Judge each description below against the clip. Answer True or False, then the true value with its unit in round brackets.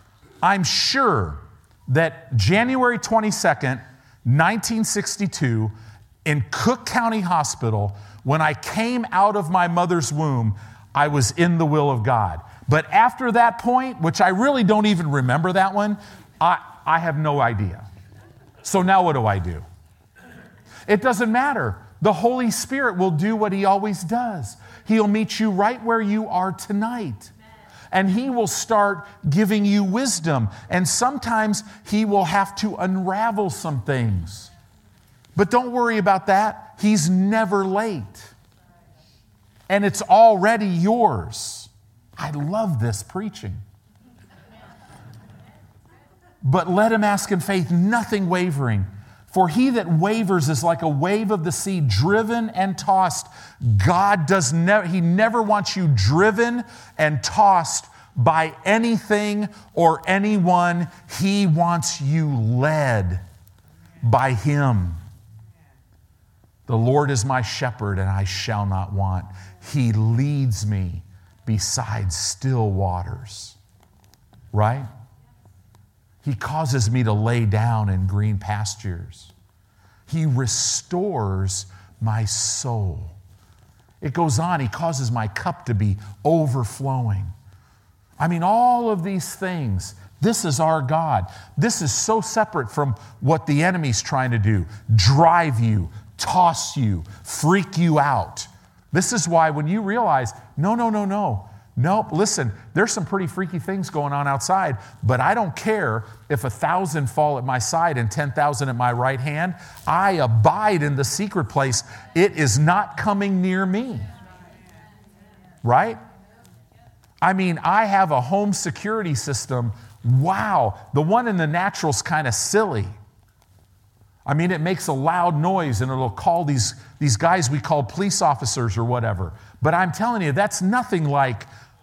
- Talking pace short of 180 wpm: True (140 wpm)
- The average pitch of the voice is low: False (145 Hz)